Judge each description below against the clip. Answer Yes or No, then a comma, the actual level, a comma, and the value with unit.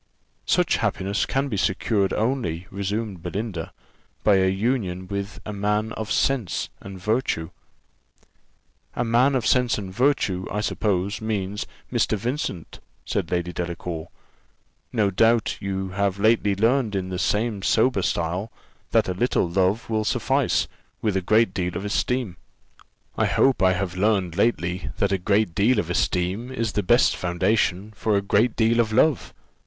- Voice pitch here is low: Yes, low, 100 Hz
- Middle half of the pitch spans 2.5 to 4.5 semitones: Yes, average, 3.3 semitones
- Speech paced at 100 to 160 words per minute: Yes, average, 155 wpm